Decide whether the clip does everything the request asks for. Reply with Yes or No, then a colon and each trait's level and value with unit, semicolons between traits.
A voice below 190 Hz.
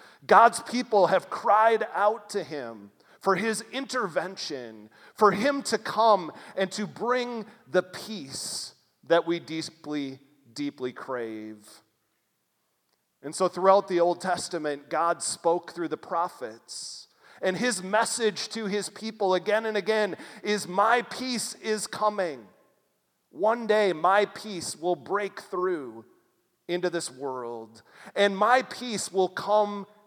No: high, 200 Hz